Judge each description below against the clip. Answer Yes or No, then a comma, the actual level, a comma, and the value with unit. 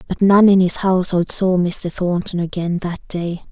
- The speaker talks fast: No, average, 190 wpm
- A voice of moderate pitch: Yes, medium, 180 Hz